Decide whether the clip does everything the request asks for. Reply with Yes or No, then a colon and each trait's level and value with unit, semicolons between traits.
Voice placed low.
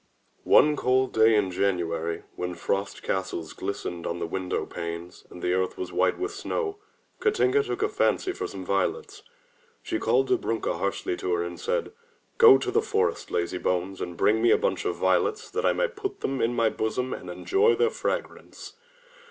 Yes: low, 125 Hz